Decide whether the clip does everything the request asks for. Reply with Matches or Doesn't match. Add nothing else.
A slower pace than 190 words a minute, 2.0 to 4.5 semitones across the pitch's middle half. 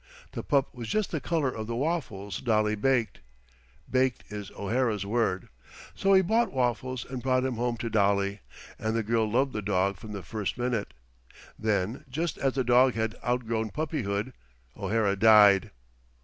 Matches